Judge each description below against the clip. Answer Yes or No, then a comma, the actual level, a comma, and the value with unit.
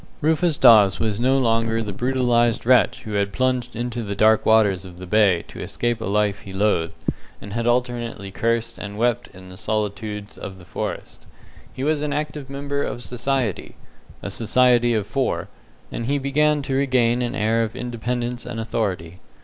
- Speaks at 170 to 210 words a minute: Yes, average, 180 wpm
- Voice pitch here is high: No, low, 115 Hz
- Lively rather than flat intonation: No, average, 3.4 semitones